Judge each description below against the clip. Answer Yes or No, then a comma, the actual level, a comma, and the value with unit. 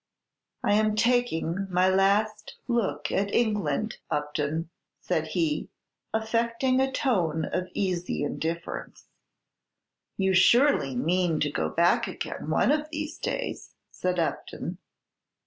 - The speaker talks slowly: Yes, slow, 115 wpm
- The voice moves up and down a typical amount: No, wide, 5.7 semitones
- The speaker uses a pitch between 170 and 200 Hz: Yes, high, 190 Hz